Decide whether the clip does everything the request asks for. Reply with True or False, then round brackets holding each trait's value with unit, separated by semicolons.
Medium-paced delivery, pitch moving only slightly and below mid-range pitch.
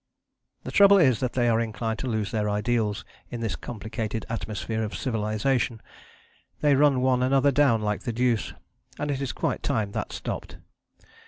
False (170 wpm; 3.2 semitones; 115 Hz)